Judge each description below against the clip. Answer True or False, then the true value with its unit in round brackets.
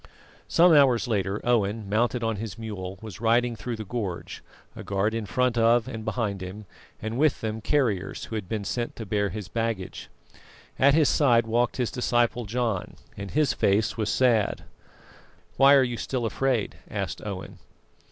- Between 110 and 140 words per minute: False (170 wpm)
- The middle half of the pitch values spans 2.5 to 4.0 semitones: True (2.8 semitones)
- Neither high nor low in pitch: False (115 Hz)